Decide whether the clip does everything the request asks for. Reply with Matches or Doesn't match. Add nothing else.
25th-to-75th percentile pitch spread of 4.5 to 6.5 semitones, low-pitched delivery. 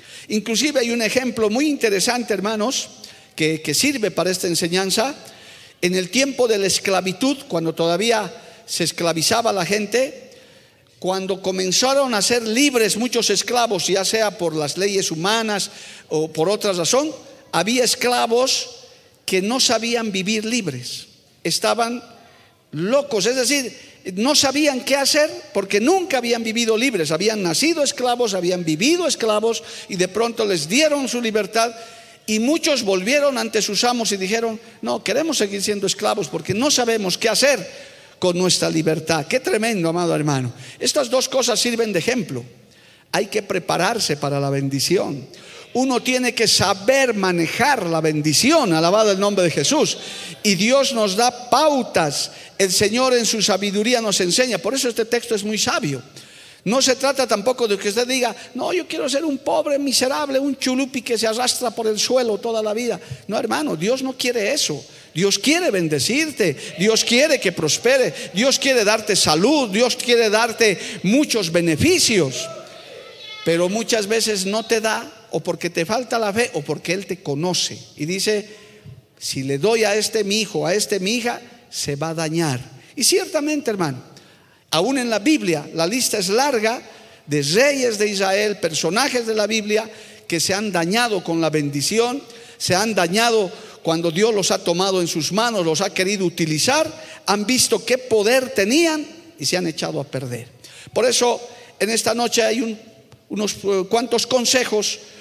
Doesn't match